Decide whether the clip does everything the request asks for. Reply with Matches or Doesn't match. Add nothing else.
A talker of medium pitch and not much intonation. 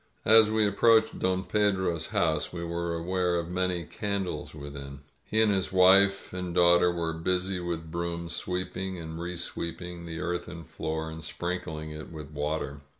Doesn't match